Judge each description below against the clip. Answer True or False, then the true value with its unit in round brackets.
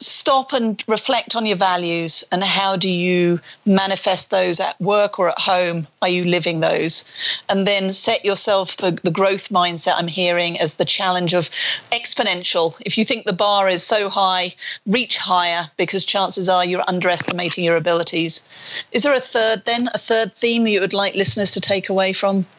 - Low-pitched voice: False (190 Hz)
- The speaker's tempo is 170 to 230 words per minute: True (185 wpm)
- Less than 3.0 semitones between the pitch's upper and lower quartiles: True (2.5 semitones)